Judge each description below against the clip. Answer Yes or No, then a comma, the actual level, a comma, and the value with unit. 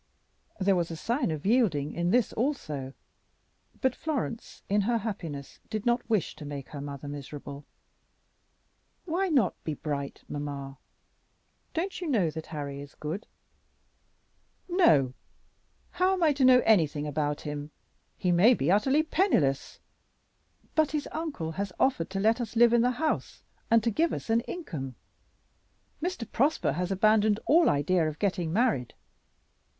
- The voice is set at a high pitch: Yes, high, 195 Hz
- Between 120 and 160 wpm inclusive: Yes, average, 150 wpm